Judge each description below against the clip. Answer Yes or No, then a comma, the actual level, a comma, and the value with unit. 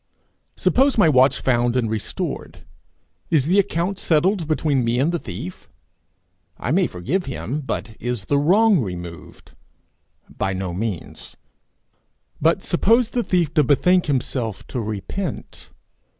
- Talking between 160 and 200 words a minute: No, slow, 135 wpm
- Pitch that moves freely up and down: Yes, wide, 7.8 semitones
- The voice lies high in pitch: No, medium, 140 Hz